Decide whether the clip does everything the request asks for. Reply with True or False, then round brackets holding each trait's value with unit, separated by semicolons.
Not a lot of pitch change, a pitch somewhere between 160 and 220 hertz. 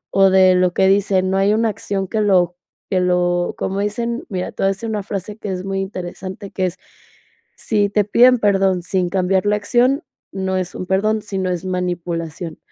True (2.1 semitones; 190 Hz)